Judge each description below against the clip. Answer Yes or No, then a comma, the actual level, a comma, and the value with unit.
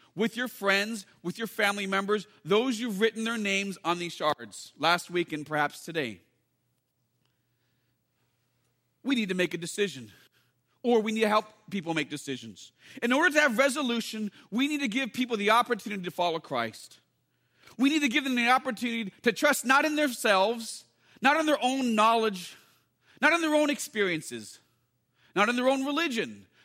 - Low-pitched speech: No, high, 205 Hz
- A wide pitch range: Yes, wide, 8.6 semitones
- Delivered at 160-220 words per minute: Yes, average, 170 wpm